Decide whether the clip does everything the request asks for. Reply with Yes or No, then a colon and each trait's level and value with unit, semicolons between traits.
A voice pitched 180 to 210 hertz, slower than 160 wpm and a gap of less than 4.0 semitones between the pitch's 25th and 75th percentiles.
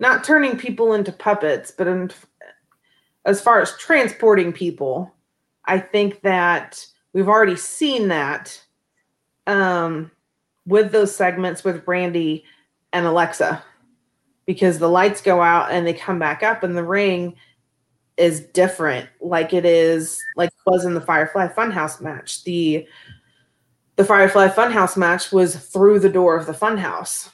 Yes: medium, 185 Hz; average, 145 wpm; average, 2.9 semitones